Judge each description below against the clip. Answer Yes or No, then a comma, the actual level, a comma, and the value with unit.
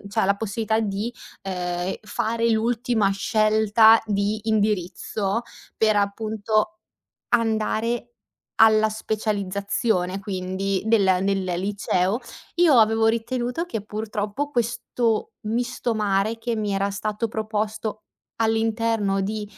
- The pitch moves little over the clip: Yes, narrow, 2.0 semitones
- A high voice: Yes, high, 215 Hz